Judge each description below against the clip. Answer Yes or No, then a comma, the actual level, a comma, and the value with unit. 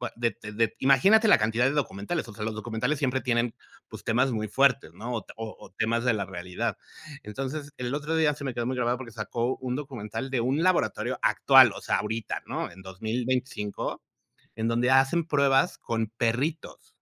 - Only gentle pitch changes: No, average, 3.4 semitones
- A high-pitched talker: No, low, 120 Hz